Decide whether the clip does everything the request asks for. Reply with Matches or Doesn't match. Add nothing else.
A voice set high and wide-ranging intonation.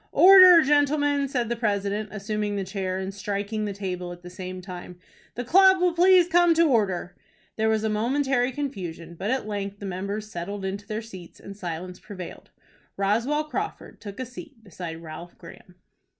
Matches